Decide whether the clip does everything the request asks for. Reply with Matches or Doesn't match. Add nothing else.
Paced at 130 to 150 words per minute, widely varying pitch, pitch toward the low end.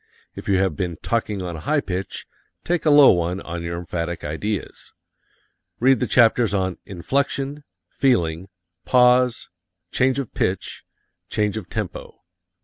Matches